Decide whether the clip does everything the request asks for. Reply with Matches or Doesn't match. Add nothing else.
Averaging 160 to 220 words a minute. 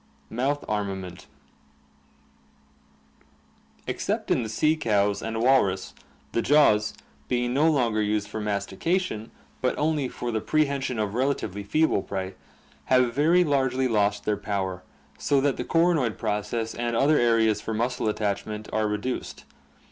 Doesn't match